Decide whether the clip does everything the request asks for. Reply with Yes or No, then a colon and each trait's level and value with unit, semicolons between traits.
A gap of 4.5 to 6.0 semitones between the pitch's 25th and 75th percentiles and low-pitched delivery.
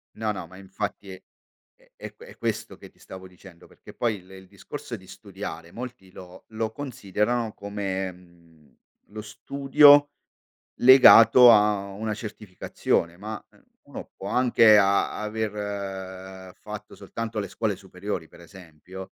No: average, 2.9 semitones; low, 100 Hz